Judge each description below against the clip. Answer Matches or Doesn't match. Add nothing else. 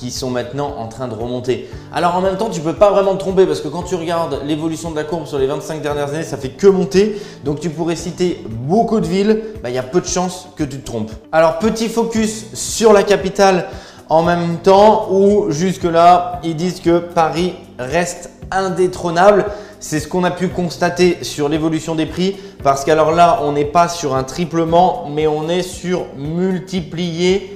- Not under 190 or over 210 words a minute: Matches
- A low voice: Doesn't match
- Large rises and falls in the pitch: Doesn't match